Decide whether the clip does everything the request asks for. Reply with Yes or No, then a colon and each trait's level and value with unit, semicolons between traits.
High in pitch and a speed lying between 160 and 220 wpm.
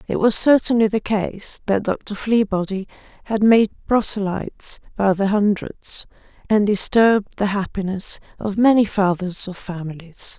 No: high, 205 Hz; slow, 135 wpm